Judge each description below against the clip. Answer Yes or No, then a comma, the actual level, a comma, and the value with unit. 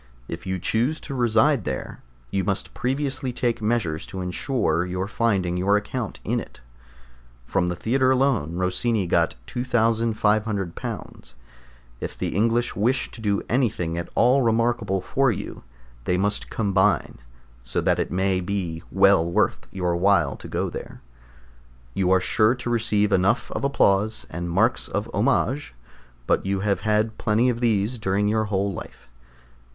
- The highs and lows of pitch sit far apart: No, average, 4.1 semitones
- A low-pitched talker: Yes, low, 105 Hz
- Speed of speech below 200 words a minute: Yes, average, 155 wpm